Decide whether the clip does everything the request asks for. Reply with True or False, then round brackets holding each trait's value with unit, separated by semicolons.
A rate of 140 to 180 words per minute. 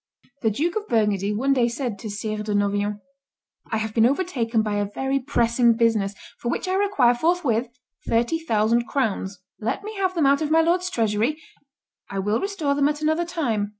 False (190 wpm)